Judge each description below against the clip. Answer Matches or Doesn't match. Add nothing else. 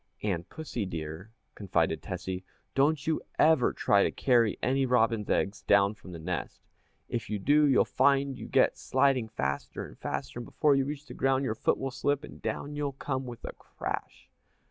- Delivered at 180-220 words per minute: Matches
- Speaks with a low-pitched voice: Matches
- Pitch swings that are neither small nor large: Doesn't match